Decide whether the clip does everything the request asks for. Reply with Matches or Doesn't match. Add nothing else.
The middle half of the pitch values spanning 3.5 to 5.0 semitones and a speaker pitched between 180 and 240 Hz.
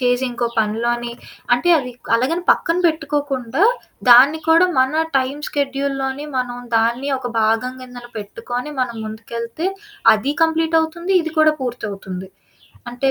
Doesn't match